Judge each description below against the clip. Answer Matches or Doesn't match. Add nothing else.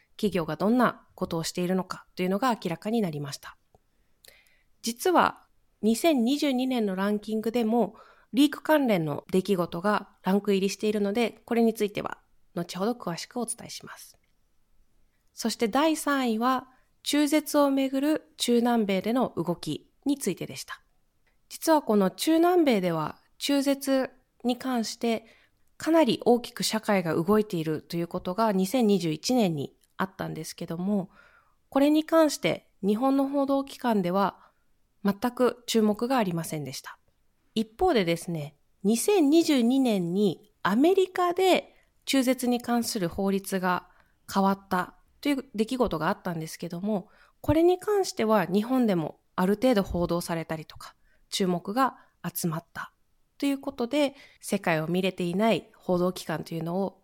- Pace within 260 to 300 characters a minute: Matches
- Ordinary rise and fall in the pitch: Doesn't match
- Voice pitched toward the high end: Matches